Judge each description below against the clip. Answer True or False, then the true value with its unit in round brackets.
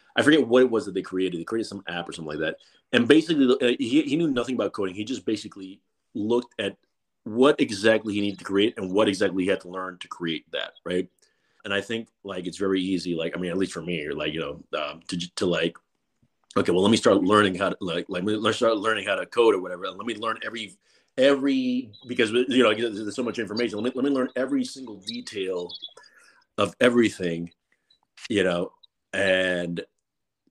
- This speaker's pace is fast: True (220 wpm)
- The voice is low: True (110 Hz)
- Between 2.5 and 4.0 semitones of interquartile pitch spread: False (5.4 semitones)